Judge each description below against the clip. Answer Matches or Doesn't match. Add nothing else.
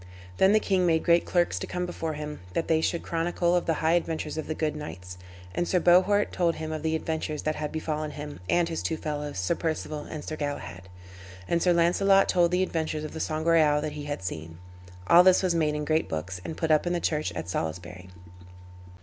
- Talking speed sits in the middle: Doesn't match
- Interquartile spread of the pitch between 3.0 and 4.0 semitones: Doesn't match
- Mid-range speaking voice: Matches